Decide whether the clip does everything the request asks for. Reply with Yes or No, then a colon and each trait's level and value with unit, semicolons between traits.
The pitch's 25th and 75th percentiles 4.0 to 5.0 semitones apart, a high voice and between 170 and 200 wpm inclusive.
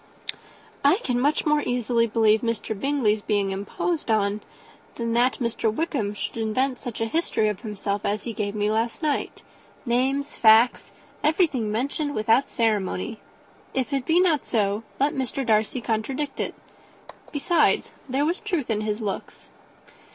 No: average, 4.6 semitones; high, 235 Hz; average, 150 wpm